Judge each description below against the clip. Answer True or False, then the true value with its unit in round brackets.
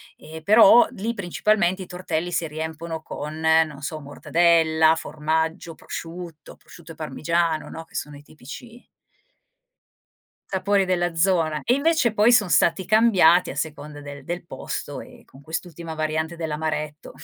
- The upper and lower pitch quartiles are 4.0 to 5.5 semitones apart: False (2.7 semitones)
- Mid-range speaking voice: True (165 Hz)